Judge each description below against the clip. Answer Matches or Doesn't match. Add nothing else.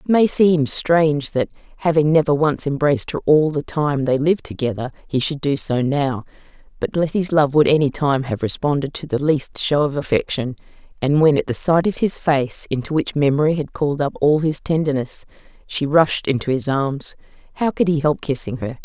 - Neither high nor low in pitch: Matches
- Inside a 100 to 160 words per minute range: Doesn't match